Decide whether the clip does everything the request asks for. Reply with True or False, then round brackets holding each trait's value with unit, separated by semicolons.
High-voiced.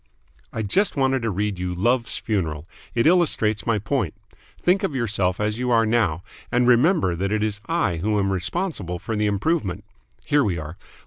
False (110 Hz)